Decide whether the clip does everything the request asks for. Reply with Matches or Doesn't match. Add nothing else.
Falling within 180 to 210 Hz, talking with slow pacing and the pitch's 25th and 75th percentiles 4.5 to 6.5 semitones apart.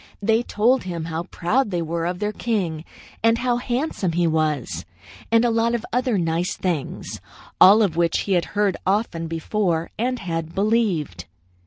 Doesn't match